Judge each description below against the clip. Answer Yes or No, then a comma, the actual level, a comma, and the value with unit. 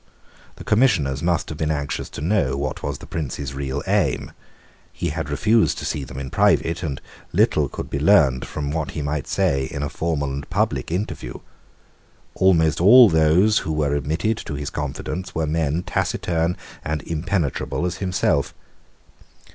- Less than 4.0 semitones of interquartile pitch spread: Yes, average, 3.6 semitones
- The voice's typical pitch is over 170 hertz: No, very low, 75 Hz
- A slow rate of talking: No, average, 165 wpm